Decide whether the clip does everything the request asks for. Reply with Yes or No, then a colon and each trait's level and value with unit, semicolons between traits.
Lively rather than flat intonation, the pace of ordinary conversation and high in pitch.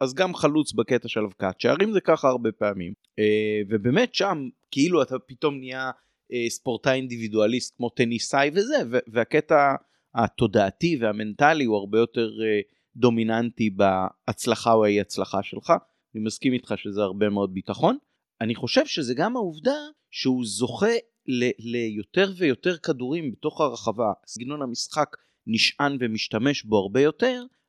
No: wide, 5.9 semitones; average, 130 wpm; low, 125 Hz